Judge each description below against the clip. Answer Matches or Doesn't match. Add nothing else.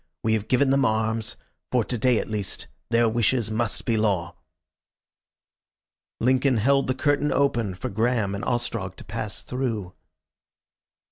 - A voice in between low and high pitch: Doesn't match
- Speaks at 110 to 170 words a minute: Matches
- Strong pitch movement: Doesn't match